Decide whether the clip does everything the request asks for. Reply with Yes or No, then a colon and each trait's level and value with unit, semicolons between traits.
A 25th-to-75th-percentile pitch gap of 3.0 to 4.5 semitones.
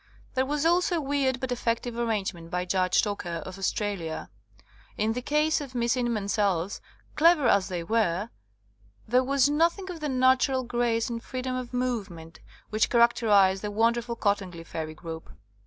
No: average, 5.0 semitones